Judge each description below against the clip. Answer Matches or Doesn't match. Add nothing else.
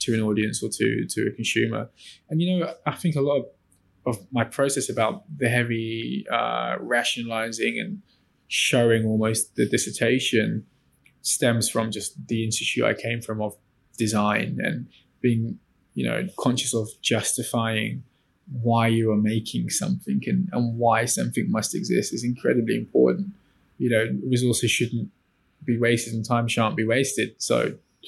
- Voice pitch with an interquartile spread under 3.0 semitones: Matches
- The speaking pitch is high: Doesn't match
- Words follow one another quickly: Doesn't match